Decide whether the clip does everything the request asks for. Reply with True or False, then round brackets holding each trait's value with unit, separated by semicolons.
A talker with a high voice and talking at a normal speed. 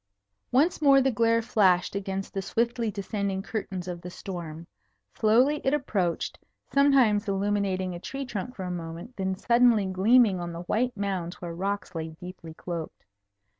True (195 Hz; 160 wpm)